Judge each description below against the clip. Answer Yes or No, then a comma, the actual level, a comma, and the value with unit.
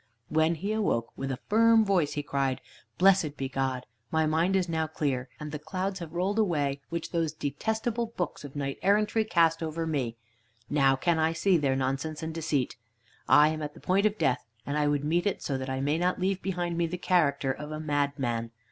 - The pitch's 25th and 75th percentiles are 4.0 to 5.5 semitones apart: Yes, average, 4.3 semitones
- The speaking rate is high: Yes, fast, 215 wpm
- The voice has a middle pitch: Yes, medium, 155 Hz